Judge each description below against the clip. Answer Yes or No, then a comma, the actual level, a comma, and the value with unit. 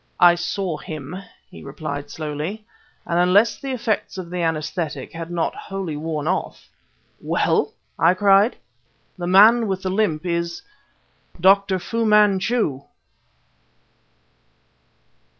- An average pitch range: Yes, average, 3.6 semitones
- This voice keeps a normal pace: No, slow, 120 wpm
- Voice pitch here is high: No, medium, 180 Hz